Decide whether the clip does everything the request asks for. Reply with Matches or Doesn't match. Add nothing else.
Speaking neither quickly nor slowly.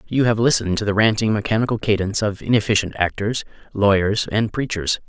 Matches